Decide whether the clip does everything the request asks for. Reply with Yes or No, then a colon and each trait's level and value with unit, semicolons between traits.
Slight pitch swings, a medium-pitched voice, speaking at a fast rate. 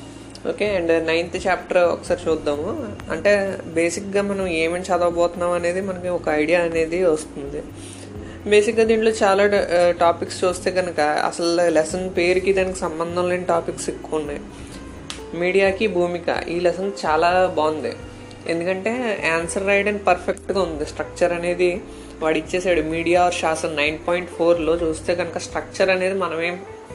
Yes: narrow, 2.2 semitones; medium, 175 Hz; fast, 130 wpm